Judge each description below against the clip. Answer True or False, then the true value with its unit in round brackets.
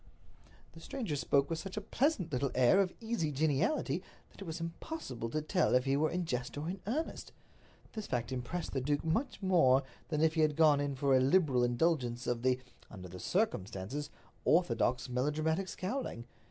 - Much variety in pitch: True (5.7 semitones)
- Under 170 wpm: False (180 wpm)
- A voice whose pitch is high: False (150 Hz)